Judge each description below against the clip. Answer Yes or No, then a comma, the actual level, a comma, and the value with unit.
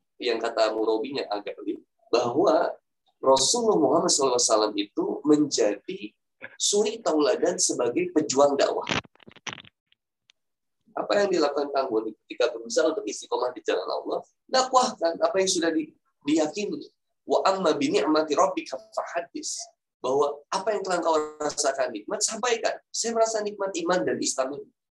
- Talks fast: No, average, 120 wpm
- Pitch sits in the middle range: Yes, medium, 180 Hz